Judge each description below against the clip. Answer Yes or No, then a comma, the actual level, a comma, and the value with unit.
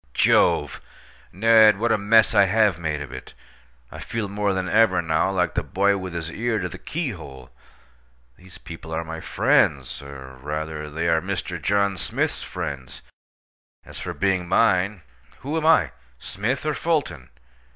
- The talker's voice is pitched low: Yes, very low, 90 Hz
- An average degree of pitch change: Yes, average, 4.9 semitones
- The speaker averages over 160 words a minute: No, average, 155 wpm